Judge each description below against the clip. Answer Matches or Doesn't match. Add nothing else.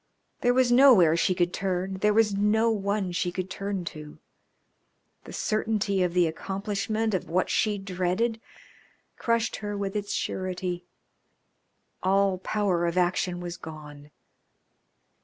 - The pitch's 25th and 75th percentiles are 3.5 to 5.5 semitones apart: Doesn't match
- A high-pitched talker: Matches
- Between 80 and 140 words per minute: Matches